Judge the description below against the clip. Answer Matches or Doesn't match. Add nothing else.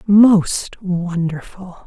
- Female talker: Matches